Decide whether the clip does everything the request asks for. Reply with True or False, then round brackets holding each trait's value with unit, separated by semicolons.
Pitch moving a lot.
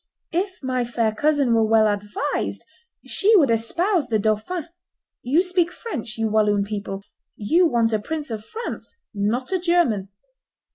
True (8.0 semitones)